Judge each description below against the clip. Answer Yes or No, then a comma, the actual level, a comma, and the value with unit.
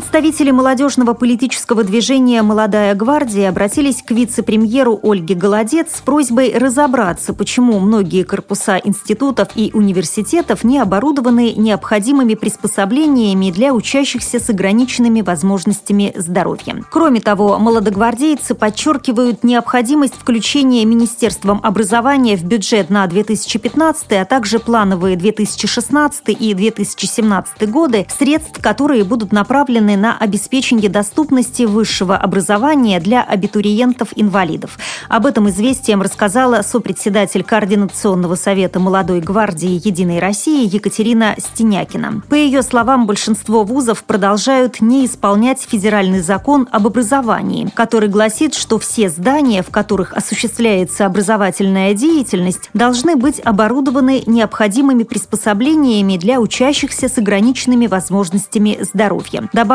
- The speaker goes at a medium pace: No, slow, 105 wpm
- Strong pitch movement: No, average, 3.7 semitones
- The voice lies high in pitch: Yes, high, 220 Hz